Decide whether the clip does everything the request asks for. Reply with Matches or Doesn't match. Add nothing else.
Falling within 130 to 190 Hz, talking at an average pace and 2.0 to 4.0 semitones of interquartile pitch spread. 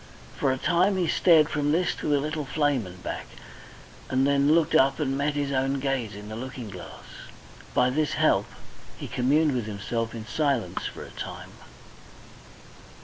Matches